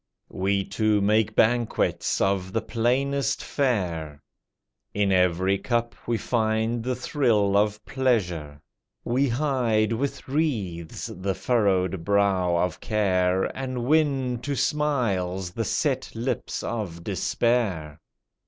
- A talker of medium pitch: No, low, 110 Hz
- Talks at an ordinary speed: No, slow, 115 wpm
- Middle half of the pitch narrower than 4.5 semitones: No, average, 4.9 semitones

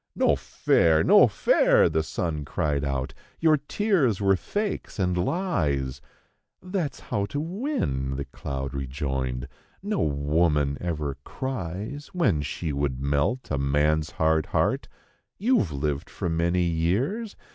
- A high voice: No, very low, 80 Hz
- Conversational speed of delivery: No, slow, 130 wpm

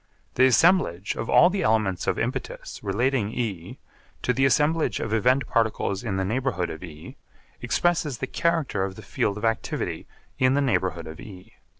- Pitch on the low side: Yes, low, 115 Hz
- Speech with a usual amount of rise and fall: No, wide, 5.9 semitones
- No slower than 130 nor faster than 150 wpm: No, average, 175 wpm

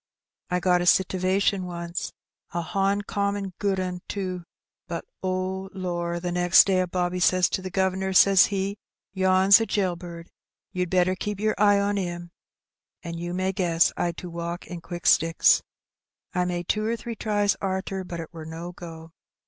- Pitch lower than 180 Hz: No, medium, 185 Hz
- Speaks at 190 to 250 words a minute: No, average, 175 wpm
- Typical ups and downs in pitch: No, narrow, 1.9 semitones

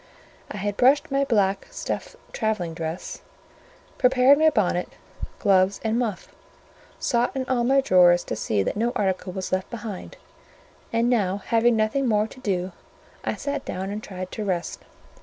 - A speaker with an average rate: Yes, average, 160 wpm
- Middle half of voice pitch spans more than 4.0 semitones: Yes, average, 4.6 semitones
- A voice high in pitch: Yes, high, 210 Hz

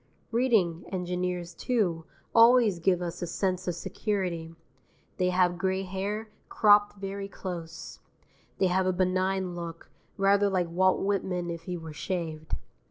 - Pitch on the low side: No, medium, 185 Hz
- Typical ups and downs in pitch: No, narrow, 2.2 semitones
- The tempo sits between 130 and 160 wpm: Yes, average, 140 wpm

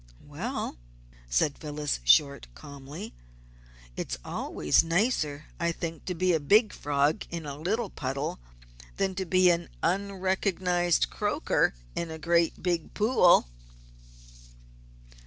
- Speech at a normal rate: No, slow, 120 wpm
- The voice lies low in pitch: No, medium, 170 Hz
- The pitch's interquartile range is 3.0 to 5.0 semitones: Yes, average, 4.1 semitones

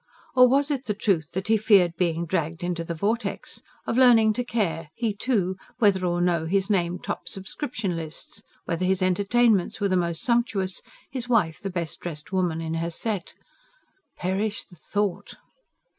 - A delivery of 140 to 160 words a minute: No, average, 175 wpm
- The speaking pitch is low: No, high, 190 Hz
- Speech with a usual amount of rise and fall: Yes, average, 4.4 semitones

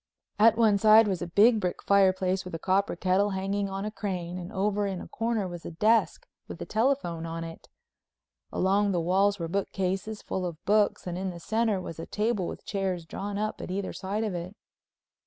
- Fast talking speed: Yes, fast, 210 wpm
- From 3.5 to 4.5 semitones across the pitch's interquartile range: No, narrow, 2.5 semitones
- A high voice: Yes, high, 195 Hz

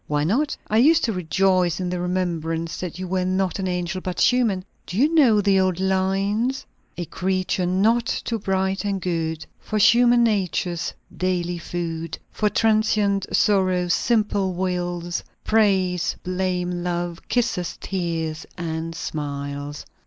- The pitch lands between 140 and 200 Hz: Yes, medium, 185 Hz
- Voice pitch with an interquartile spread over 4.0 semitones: No, average, 2.8 semitones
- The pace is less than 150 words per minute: Yes, average, 140 wpm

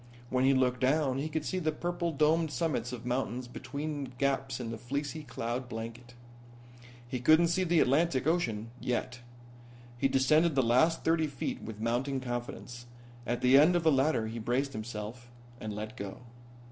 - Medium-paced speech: Yes, average, 170 wpm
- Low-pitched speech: Yes, low, 130 Hz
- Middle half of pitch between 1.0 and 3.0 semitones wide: No, average, 4.2 semitones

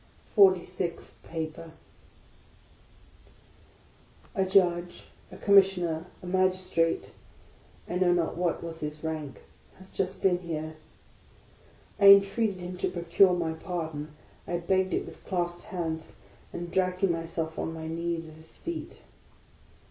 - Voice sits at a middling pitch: Yes, medium, 175 Hz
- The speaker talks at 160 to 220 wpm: No, slow, 135 wpm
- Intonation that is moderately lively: No, narrow, 2.3 semitones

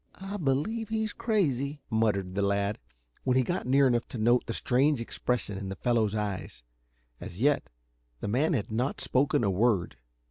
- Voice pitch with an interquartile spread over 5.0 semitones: Yes, wide, 5.5 semitones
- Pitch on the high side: No, low, 120 Hz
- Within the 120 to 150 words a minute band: No, average, 175 wpm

